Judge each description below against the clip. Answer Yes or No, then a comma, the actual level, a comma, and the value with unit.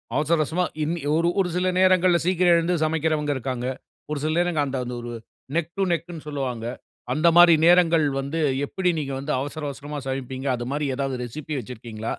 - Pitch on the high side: No, medium, 150 Hz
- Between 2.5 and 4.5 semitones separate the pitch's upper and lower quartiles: Yes, average, 3.9 semitones